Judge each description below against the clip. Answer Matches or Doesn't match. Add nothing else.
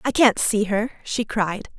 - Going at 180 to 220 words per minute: Matches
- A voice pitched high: Matches